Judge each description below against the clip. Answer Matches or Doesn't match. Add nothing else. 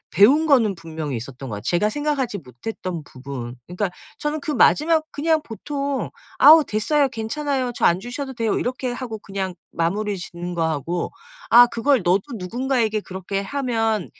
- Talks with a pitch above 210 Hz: Matches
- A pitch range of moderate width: Doesn't match